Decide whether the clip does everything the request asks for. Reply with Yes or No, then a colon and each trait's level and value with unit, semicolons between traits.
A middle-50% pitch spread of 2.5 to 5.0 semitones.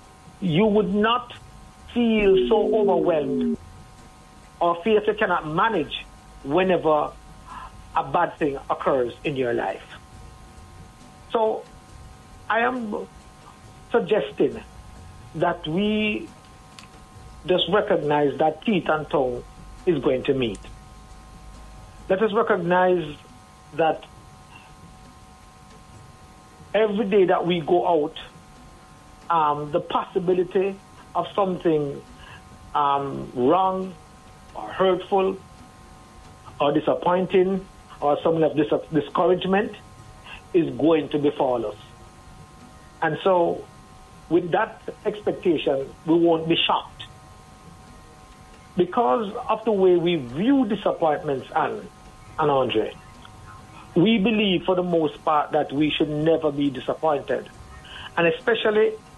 No: wide, 5.6 semitones